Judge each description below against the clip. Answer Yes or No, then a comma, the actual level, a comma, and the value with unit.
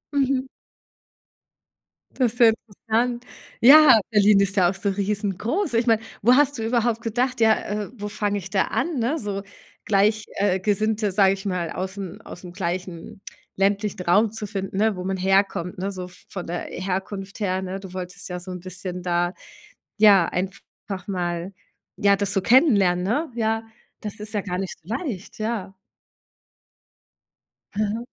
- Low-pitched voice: No, high, 200 Hz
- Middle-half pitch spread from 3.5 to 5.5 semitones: No, average, 3.1 semitones